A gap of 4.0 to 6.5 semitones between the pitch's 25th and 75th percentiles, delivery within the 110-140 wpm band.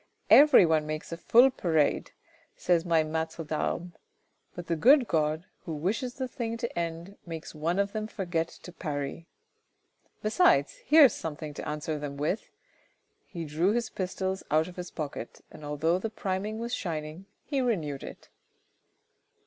No: wide, 5.5 semitones; average, 160 wpm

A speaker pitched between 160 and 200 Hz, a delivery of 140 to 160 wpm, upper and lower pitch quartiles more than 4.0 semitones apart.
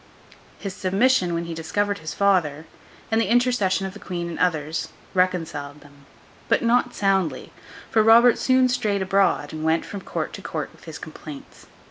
No: high, 190 Hz; average, 170 wpm; average, 5.2 semitones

